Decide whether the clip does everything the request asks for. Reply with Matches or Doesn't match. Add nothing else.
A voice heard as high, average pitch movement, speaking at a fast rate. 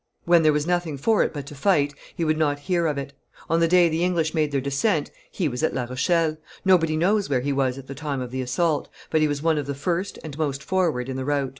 Doesn't match